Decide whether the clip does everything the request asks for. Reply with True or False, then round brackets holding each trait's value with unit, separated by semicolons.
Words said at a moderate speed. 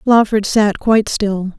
True (150 wpm)